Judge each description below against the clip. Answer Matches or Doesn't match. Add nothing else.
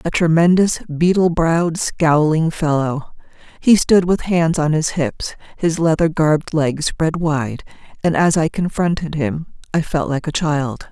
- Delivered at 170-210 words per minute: Doesn't match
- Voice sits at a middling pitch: Matches